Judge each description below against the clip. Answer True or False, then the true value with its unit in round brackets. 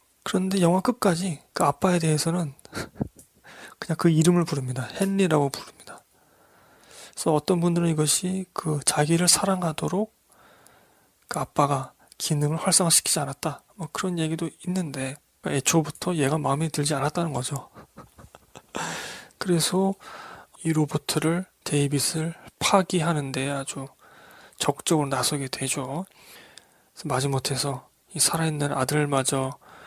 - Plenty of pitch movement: False (3.7 semitones)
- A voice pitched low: False (155 Hz)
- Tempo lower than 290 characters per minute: True (280 characters per minute)